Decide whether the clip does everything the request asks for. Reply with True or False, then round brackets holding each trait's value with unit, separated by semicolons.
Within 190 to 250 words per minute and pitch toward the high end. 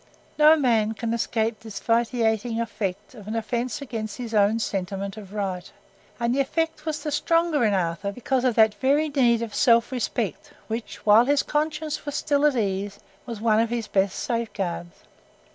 False (180 wpm; 230 Hz)